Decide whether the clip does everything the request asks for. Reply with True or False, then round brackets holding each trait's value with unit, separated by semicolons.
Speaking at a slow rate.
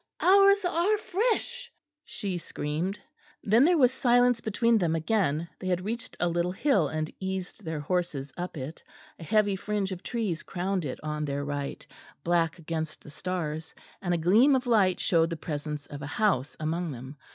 False (175 wpm)